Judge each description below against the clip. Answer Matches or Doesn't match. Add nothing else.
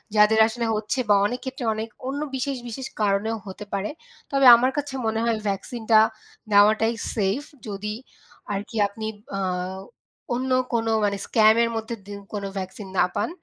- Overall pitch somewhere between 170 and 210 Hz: Doesn't match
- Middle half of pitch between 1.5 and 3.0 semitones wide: Matches